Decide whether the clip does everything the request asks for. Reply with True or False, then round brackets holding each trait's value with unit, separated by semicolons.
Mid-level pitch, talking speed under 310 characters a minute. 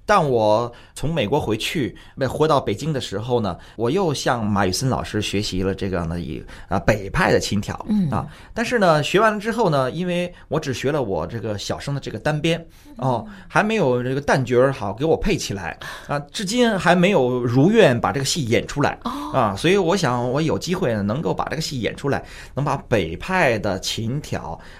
False (125 Hz; 285 characters per minute)